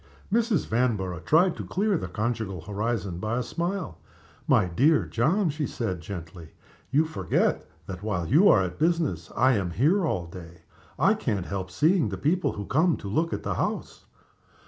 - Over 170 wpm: Yes, average, 180 wpm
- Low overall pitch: Yes, low, 110 Hz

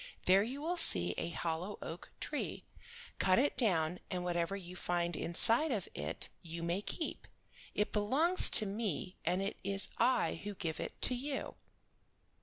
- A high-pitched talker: Yes, high, 195 Hz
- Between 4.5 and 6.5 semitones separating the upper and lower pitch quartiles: Yes, average, 5.2 semitones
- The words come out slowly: No, average, 165 wpm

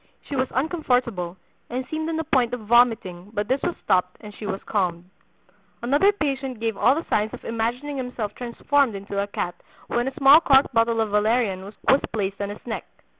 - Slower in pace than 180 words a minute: No, average, 195 wpm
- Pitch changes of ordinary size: Yes, average, 4.6 semitones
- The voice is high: Yes, high, 235 Hz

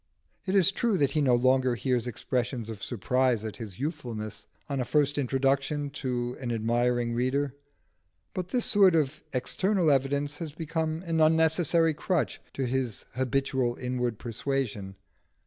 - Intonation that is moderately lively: Yes, average, 4.2 semitones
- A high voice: No, low, 135 Hz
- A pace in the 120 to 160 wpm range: Yes, average, 145 wpm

